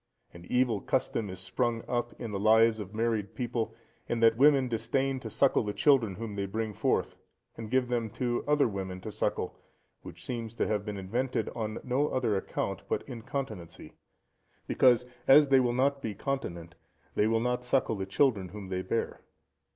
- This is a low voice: Yes, low, 115 Hz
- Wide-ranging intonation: No, average, 3.6 semitones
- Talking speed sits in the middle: Yes, average, 180 wpm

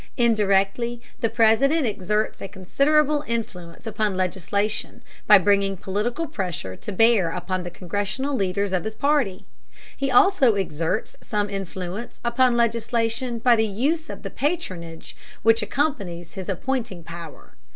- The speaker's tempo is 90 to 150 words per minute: Yes, slow, 135 wpm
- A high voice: Yes, high, 210 Hz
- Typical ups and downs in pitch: Yes, average, 4.2 semitones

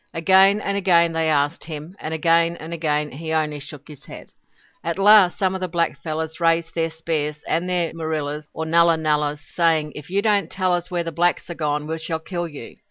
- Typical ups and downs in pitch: No, narrow, 2.2 semitones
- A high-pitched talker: No, medium, 165 Hz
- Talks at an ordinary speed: No, fast, 220 wpm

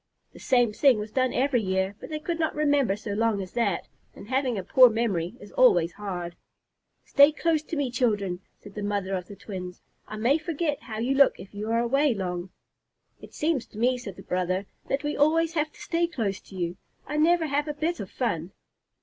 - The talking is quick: Yes, fast, 220 wpm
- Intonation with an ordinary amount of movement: No, wide, 6.7 semitones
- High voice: Yes, high, 235 Hz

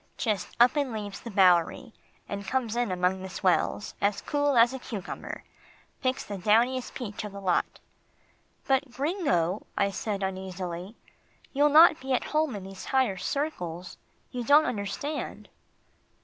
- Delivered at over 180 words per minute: No, average, 150 wpm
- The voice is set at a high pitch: Yes, high, 215 Hz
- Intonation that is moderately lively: No, wide, 5.7 semitones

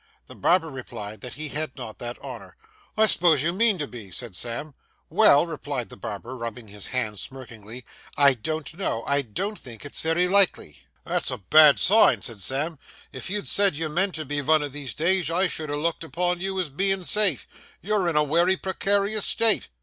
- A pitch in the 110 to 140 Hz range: No, medium, 155 Hz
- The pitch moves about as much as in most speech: No, wide, 6.4 semitones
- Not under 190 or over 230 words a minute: Yes, average, 200 wpm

